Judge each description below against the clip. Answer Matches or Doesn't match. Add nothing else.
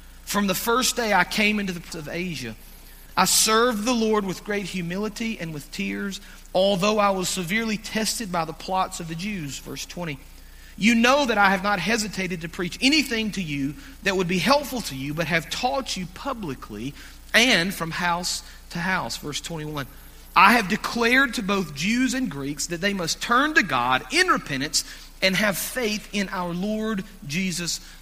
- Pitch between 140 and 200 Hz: Matches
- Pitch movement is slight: Doesn't match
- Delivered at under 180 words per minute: Doesn't match